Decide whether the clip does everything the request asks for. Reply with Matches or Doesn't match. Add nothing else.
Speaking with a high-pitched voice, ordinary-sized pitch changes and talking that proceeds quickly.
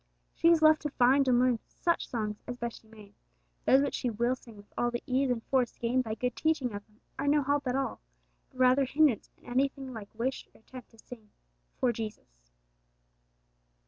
Matches